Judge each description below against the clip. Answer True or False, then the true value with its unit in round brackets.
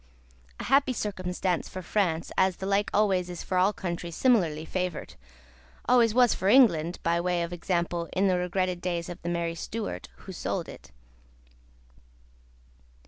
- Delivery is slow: False (155 wpm)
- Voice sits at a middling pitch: True (180 Hz)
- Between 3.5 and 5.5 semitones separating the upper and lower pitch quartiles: False (2.7 semitones)